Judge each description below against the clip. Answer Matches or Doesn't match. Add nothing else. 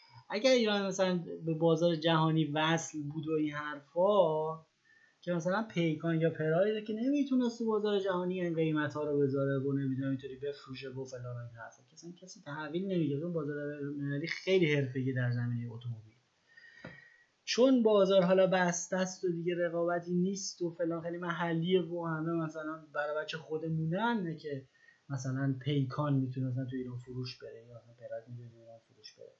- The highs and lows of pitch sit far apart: Doesn't match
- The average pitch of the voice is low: Doesn't match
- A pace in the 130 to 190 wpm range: Matches